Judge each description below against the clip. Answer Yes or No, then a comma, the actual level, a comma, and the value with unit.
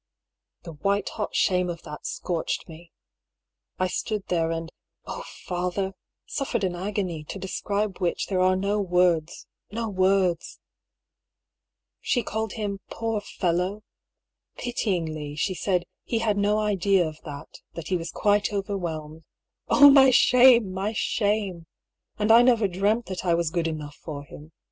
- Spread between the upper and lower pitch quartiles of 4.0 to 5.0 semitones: No, average, 3.6 semitones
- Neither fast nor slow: Yes, average, 165 wpm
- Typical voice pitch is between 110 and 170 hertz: No, high, 190 Hz